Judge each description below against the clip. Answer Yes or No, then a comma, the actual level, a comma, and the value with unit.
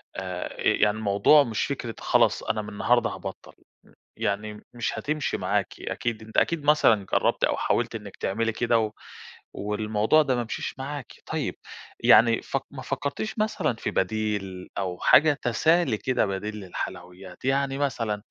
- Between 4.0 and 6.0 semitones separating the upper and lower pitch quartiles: Yes, average, 4.8 semitones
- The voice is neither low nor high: No, low, 115 Hz